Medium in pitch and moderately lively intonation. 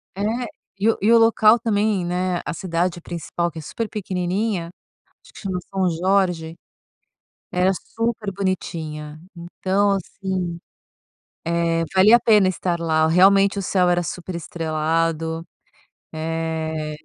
Yes: medium, 180 Hz; average, 3.0 semitones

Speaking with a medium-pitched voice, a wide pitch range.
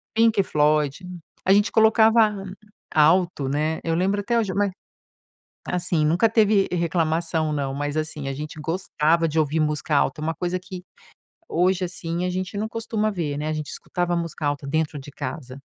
No: medium, 165 Hz; average, 3.9 semitones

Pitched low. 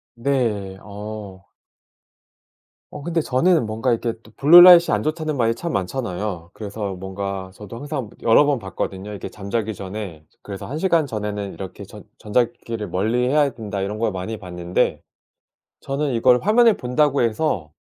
Yes: low, 110 Hz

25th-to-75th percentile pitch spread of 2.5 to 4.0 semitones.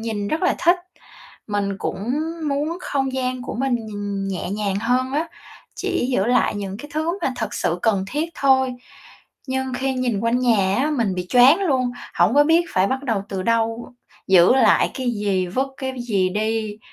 No: average, 4.6 semitones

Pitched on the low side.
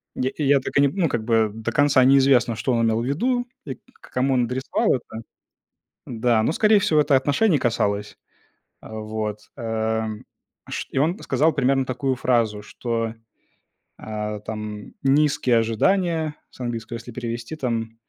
Yes: low, 125 Hz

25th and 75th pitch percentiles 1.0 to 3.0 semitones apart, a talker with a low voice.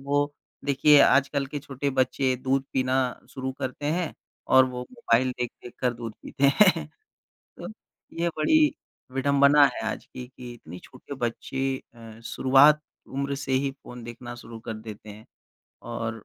Yes: average, 2.7 semitones; low, 130 Hz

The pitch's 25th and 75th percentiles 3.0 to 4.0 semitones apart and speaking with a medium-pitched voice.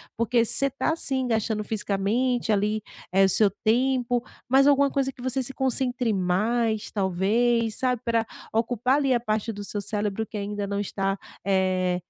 No: average, 3.5 semitones; high, 225 Hz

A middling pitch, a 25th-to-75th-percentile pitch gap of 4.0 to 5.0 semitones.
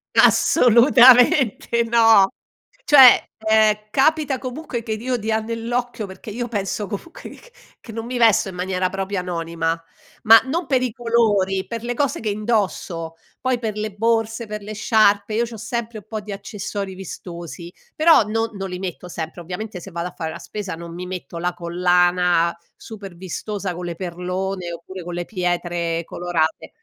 No: high, 205 Hz; average, 4.4 semitones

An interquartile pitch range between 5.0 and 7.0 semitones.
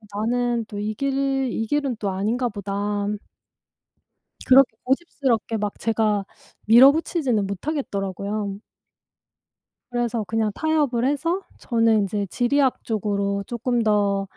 No: average, 4.3 semitones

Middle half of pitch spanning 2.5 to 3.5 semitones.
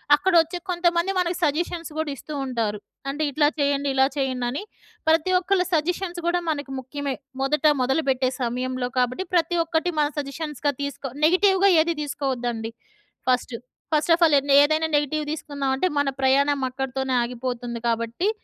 No: average, 4.0 semitones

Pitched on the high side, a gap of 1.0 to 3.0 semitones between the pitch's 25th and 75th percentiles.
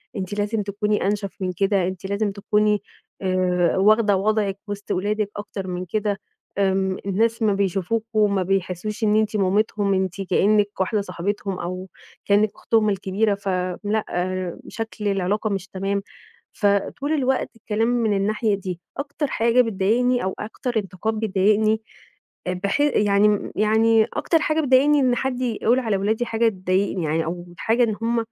Yes: high, 205 Hz; narrow, 2.5 semitones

